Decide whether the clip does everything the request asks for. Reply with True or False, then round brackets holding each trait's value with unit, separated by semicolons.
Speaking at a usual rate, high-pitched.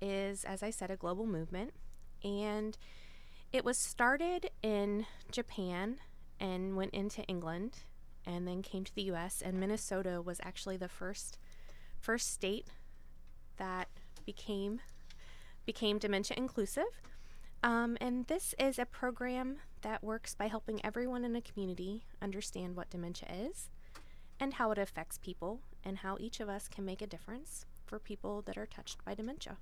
True (150 wpm; 205 Hz)